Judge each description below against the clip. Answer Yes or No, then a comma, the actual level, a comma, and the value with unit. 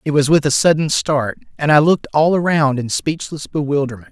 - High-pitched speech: No, medium, 145 Hz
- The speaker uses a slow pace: No, fast, 205 wpm